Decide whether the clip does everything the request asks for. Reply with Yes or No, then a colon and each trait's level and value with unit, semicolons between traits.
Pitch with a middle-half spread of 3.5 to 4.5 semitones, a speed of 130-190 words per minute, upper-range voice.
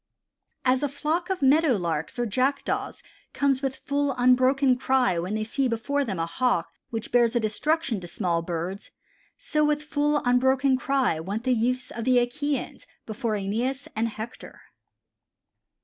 Yes: average, 4.2 semitones; average, 155 wpm; very high, 250 Hz